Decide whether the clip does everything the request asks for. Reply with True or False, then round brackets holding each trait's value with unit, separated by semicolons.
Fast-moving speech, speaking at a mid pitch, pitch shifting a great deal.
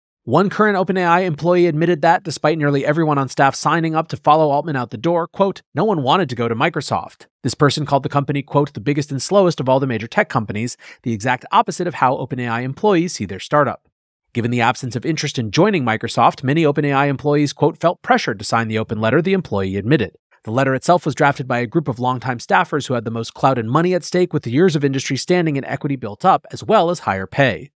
False (240 wpm; 145 Hz; 5.0 semitones)